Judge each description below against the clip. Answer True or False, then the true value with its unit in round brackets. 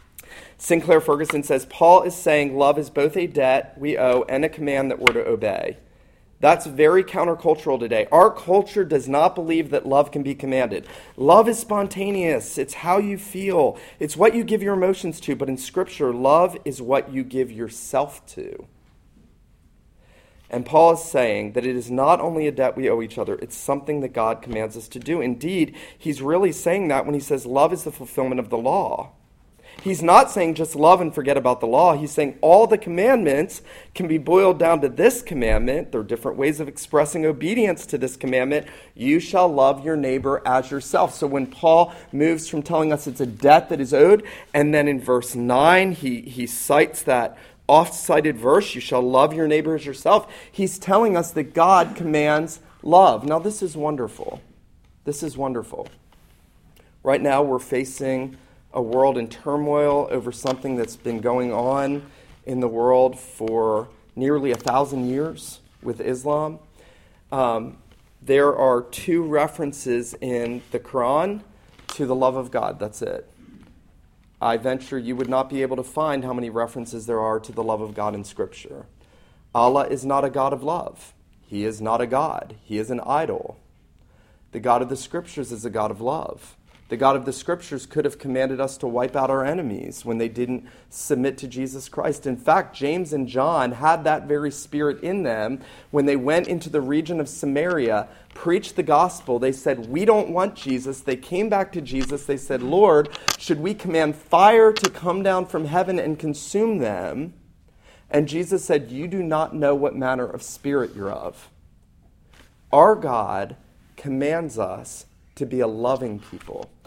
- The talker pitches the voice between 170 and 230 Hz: False (145 Hz)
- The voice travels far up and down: False (4.6 semitones)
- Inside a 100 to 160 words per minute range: False (185 wpm)